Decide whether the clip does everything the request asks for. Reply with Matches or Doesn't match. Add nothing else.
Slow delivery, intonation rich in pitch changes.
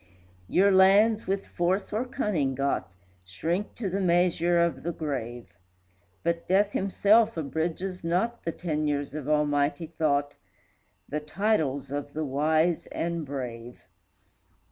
Doesn't match